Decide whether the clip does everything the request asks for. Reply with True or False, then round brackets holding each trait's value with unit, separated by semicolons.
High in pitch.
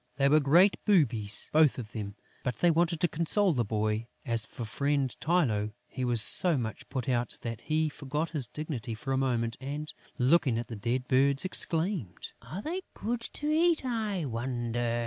False (135 Hz)